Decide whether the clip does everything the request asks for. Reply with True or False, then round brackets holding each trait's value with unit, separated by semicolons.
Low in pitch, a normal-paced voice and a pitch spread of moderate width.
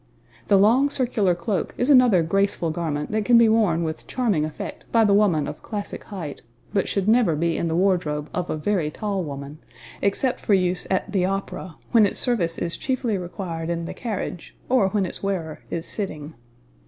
False (190 Hz; 190 wpm; 4.3 semitones)